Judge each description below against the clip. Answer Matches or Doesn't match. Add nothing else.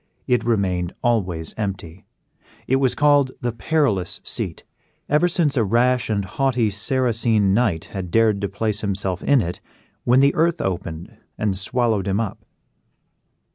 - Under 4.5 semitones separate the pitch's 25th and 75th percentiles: Doesn't match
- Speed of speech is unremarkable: Matches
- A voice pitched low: Matches